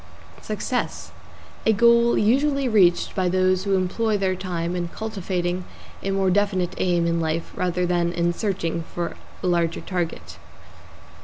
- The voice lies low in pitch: No, medium, 185 Hz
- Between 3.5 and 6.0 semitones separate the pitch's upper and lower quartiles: No, average, 2.8 semitones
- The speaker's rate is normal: Yes, average, 145 wpm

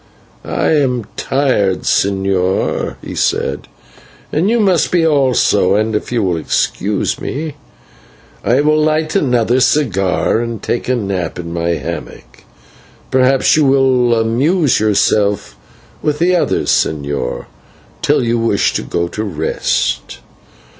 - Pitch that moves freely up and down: Yes, wide, 6.7 semitones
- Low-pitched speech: Yes, low, 115 Hz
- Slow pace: Yes, slow, 130 wpm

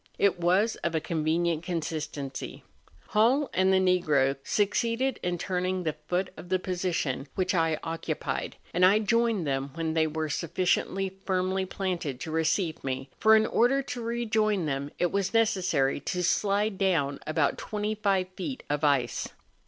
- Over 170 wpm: No, average, 160 wpm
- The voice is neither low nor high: Yes, medium, 180 Hz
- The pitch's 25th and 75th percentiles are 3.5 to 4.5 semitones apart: Yes, average, 4.2 semitones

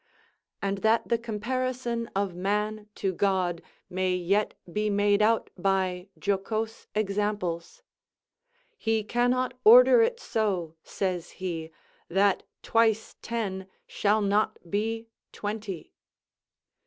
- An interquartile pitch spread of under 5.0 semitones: Yes, average, 3.0 semitones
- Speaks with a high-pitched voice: Yes, high, 210 Hz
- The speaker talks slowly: Yes, slow, 105 wpm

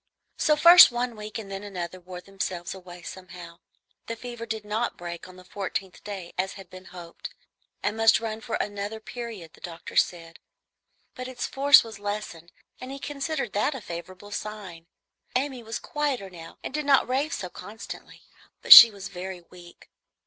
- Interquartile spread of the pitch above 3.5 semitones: Yes, average, 4.6 semitones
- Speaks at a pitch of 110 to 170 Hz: No, high, 205 Hz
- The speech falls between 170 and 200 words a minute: Yes, average, 180 wpm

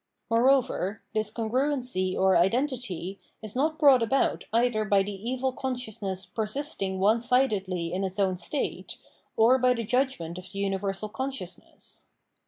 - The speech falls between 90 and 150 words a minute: Yes, average, 140 wpm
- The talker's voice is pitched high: Yes, high, 220 Hz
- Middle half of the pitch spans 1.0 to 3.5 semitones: No, average, 4.9 semitones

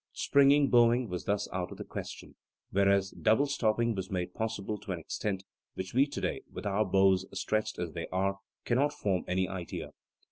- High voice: No, low, 100 Hz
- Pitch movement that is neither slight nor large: Yes, average, 3.7 semitones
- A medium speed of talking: Yes, average, 180 wpm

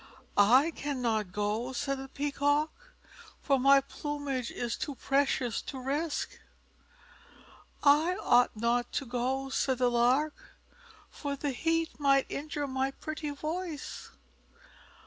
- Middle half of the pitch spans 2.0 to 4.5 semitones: Yes, narrow, 2.6 semitones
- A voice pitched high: Yes, very high, 275 Hz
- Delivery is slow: Yes, slow, 120 wpm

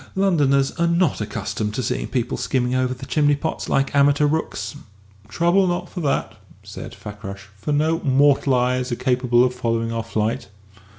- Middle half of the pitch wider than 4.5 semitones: No, average, 3.8 semitones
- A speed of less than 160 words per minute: No, average, 170 wpm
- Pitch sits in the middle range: No, low, 130 Hz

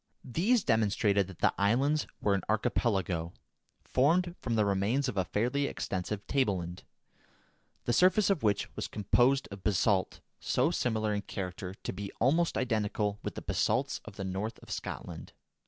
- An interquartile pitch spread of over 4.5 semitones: Yes, average, 4.9 semitones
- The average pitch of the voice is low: Yes, low, 105 Hz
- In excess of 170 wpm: No, average, 160 wpm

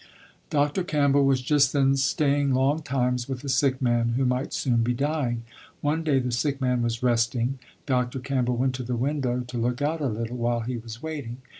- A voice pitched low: Yes, low, 130 Hz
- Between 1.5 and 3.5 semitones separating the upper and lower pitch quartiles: Yes, average, 2.7 semitones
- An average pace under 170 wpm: No, average, 200 wpm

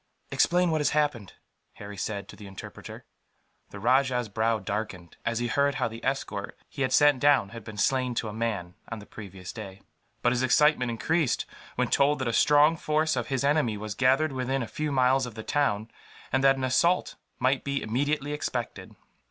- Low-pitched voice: Yes, low, 125 Hz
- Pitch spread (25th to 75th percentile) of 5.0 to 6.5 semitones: No, average, 4.5 semitones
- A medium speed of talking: Yes, average, 195 wpm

